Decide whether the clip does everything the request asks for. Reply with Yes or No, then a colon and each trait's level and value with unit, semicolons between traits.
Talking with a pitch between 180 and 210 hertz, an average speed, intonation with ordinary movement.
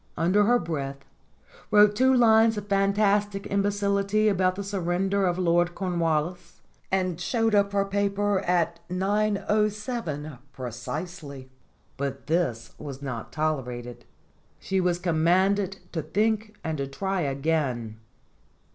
No: medium, 185 Hz; slow, 120 wpm; average, 4.6 semitones